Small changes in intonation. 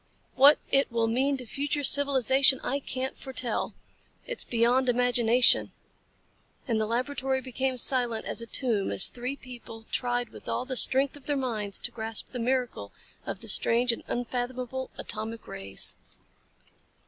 Yes: narrow, 2.3 semitones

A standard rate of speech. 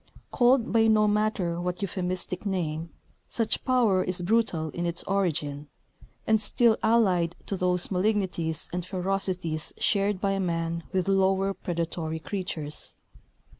No: slow, 130 wpm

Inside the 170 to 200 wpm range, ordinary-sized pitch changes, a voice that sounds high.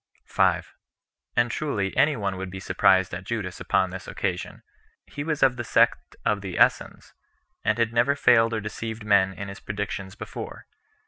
No: average, 175 wpm; average, 3.6 semitones; low, 105 Hz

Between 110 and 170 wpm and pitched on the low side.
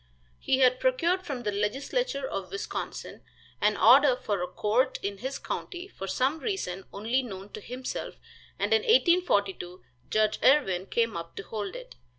No: average, 160 wpm; high, 245 Hz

